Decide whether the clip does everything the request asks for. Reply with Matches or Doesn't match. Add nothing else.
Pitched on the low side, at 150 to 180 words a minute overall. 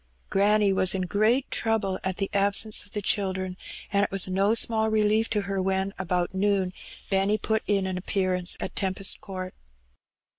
Doesn't match